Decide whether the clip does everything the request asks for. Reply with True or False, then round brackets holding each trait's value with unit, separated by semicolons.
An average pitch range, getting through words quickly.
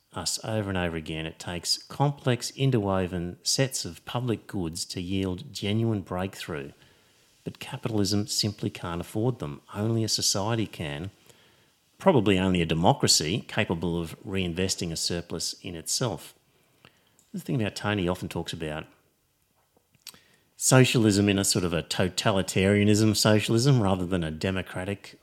False (3.9 semitones; 140 wpm)